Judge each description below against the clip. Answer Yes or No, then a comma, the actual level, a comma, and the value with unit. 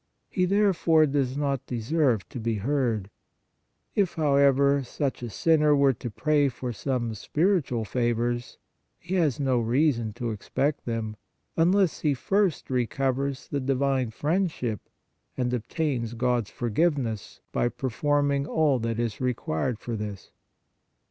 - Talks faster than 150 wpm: No, slow, 135 wpm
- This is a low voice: Yes, low, 130 Hz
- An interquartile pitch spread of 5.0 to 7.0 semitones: No, average, 3.9 semitones